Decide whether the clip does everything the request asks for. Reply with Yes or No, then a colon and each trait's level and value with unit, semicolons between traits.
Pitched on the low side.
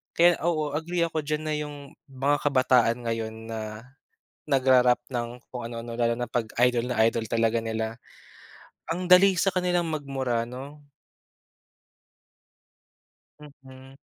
Yes: low, 130 Hz